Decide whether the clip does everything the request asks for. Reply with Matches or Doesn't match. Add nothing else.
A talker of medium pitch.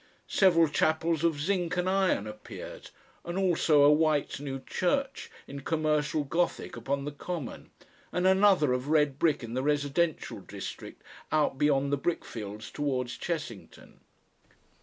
Matches